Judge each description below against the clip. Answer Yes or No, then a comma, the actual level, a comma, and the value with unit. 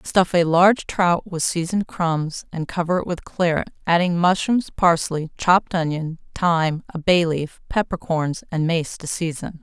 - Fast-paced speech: No, average, 170 wpm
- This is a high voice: No, medium, 170 Hz